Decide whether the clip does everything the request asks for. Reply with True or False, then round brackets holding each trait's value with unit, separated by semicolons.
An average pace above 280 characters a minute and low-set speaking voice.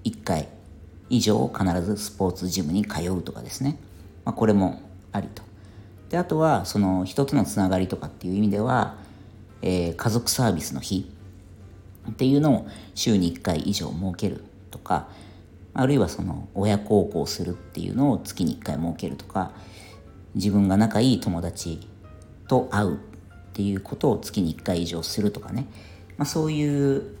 True (300 characters per minute; 100 Hz)